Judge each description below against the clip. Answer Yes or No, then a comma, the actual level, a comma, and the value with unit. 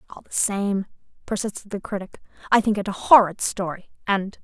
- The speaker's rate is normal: Yes, average, 175 wpm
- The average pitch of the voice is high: Yes, high, 200 Hz